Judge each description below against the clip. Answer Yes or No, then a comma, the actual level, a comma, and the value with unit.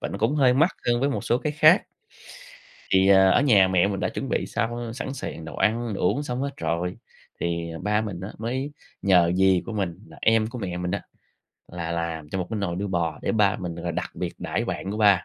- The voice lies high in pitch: No, low, 100 Hz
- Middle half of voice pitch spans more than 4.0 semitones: Yes, average, 5.1 semitones